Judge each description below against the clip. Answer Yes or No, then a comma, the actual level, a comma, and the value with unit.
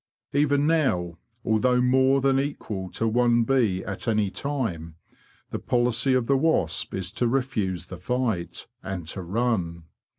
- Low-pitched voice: Yes, low, 115 Hz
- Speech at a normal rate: Yes, average, 145 wpm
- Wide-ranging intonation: Yes, wide, 6.0 semitones